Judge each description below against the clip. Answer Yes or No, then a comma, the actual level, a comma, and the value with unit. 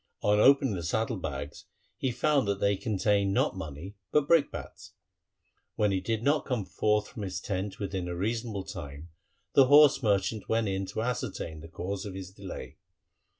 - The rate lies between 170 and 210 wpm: Yes, average, 180 wpm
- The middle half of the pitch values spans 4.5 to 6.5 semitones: No, average, 3.3 semitones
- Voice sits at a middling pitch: No, low, 100 Hz